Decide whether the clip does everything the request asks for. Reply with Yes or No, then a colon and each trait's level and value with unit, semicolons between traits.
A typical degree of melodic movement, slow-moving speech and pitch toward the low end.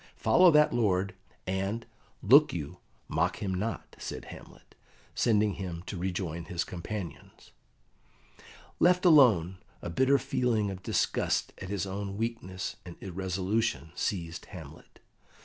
Yes: average, 4.0 semitones; slow, 125 wpm; very low, 95 Hz